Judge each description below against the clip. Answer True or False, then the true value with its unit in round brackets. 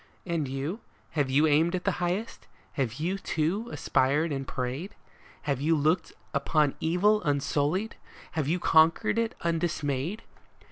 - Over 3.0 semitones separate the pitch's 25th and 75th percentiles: True (4.1 semitones)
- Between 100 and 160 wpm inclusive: True (140 wpm)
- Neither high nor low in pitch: True (160 Hz)